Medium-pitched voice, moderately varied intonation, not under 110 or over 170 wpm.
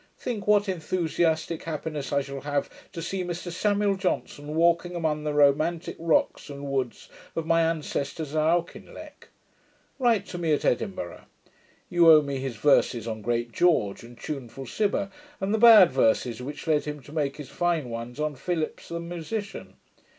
Yes: medium, 155 Hz; average, 3.9 semitones; average, 165 wpm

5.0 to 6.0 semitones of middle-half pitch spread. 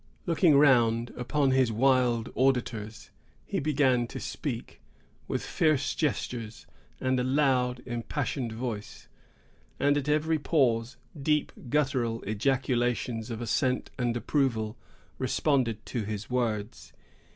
No: average, 3.1 semitones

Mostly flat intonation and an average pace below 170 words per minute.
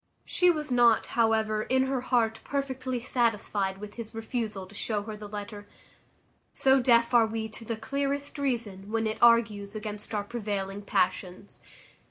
No: average, 3.0 semitones; average, 160 wpm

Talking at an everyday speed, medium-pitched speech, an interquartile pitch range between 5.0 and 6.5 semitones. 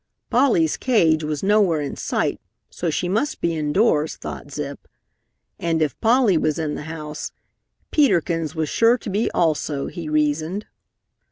Yes: average, 155 wpm; medium, 160 Hz; average, 5.3 semitones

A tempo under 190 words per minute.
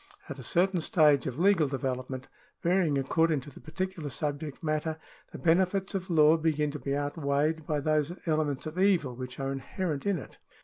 Yes: average, 180 wpm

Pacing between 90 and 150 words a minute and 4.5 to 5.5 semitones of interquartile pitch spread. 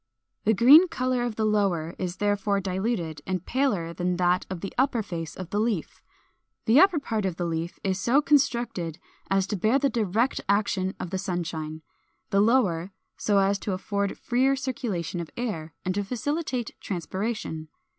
No: average, 175 wpm; average, 5.1 semitones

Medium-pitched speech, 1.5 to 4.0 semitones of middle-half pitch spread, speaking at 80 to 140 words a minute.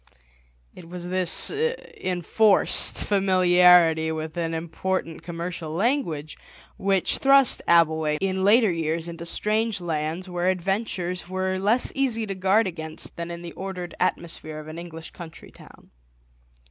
Yes: medium, 180 Hz; average, 2.8 semitones; slow, 135 wpm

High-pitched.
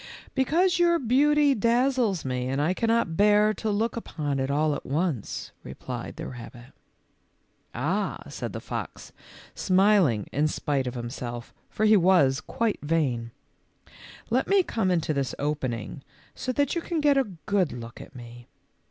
No: medium, 175 Hz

